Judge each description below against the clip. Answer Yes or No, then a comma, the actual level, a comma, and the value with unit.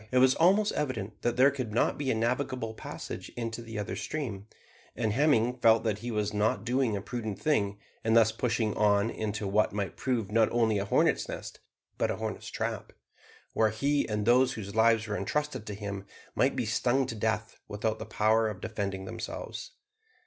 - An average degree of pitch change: Yes, average, 3.0 semitones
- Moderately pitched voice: No, low, 110 Hz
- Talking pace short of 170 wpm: No, average, 190 wpm